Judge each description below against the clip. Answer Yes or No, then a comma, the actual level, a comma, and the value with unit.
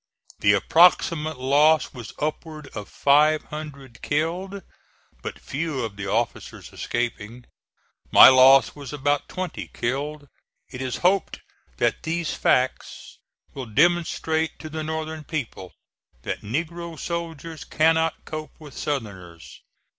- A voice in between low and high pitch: Yes, medium, 150 Hz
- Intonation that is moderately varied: Yes, average, 3.9 semitones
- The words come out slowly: Yes, slow, 120 wpm